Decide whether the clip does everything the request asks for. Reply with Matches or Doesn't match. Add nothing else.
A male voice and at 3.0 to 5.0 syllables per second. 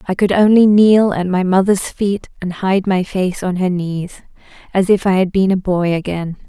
Doesn't match